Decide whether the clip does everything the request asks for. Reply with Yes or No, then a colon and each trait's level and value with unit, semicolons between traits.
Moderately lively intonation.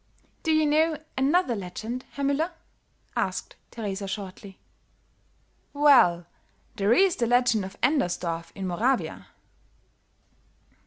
No: wide, 7.1 semitones